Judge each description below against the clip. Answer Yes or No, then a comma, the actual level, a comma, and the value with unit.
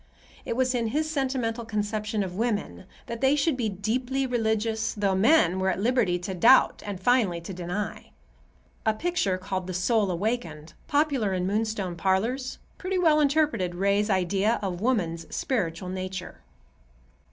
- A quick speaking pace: No, average, 150 wpm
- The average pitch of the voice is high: Yes, high, 215 Hz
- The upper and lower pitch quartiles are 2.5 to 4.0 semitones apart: No, average, 4.9 semitones